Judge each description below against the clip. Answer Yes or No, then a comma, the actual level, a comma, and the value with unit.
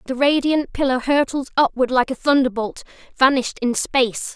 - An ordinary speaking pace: Yes, average, 165 wpm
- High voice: Yes, very high, 260 Hz